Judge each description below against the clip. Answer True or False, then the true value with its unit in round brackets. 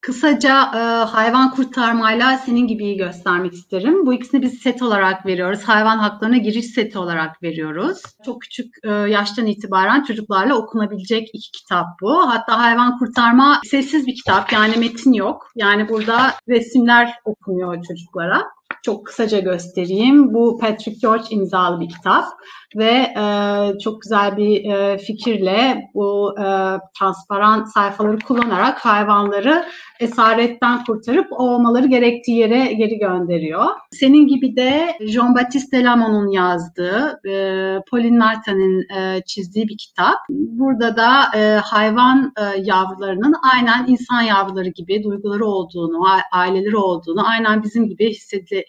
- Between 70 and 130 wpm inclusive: True (125 wpm)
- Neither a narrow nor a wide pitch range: True (3.8 semitones)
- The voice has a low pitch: False (220 Hz)